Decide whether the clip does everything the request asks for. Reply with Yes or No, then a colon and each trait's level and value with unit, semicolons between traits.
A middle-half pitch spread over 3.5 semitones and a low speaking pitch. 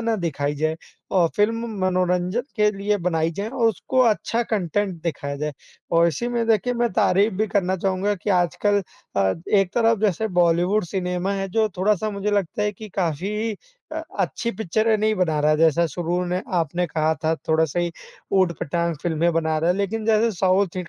No: average, 3.9 semitones; medium, 185 Hz